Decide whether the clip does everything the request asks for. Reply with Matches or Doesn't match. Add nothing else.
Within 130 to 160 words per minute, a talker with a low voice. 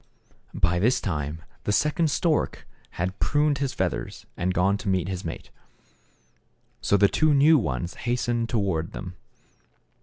Matches